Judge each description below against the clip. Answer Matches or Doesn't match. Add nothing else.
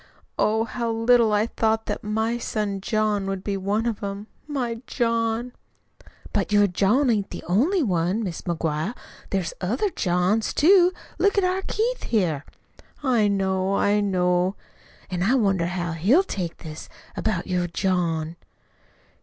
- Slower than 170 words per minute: Matches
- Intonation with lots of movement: Doesn't match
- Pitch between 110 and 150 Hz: Doesn't match